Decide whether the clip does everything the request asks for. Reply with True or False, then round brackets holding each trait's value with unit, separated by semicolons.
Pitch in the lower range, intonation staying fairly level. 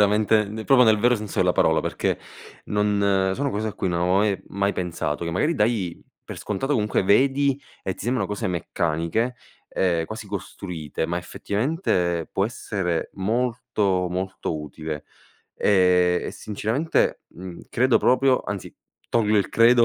False (100 Hz; 4.3 semitones)